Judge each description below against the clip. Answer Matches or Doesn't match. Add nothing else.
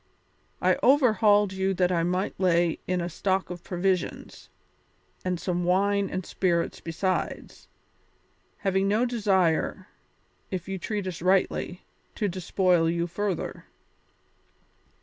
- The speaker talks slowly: Matches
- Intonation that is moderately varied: Doesn't match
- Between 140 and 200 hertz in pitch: Matches